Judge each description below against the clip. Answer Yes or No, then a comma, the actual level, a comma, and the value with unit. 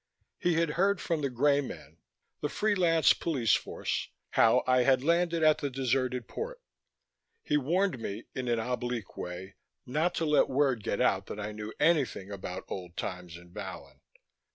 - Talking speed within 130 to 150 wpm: No, average, 170 wpm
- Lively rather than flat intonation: Yes, wide, 7.2 semitones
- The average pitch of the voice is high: No, low, 130 Hz